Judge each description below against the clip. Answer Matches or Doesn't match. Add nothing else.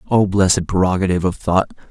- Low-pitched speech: Matches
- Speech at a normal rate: Matches